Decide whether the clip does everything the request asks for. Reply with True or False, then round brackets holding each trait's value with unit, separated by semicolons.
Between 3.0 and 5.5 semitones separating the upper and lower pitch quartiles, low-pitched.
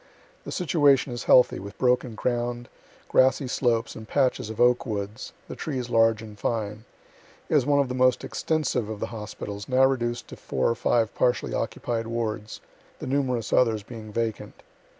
False (2.6 semitones; 120 Hz)